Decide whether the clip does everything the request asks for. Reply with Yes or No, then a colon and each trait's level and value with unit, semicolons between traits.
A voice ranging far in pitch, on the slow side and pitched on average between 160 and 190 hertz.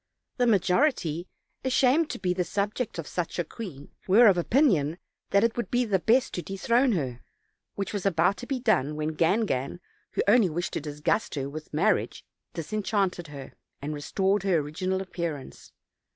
No: wide, 6.0 semitones; average, 170 wpm; medium, 185 Hz